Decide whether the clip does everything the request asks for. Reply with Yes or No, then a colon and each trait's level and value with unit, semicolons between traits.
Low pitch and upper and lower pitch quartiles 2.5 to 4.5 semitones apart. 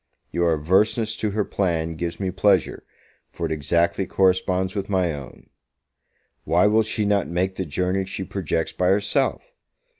Yes: very low, 95 Hz; average, 2.9 semitones